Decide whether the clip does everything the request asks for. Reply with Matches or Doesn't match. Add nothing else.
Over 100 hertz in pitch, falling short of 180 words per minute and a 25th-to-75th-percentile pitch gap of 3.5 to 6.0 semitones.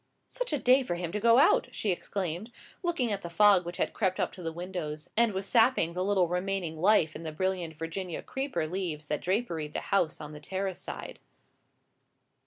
Doesn't match